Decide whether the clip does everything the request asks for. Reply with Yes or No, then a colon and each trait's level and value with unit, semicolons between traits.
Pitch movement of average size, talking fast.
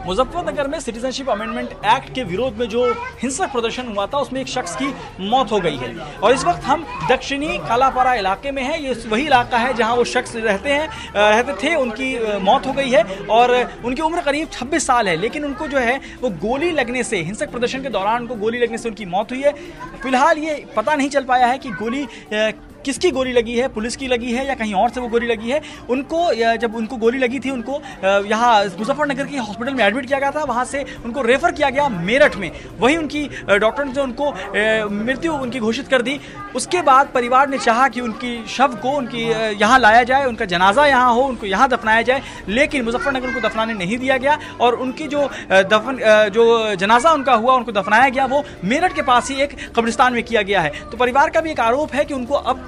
Yes: average, 3.3 semitones; fast, 220 wpm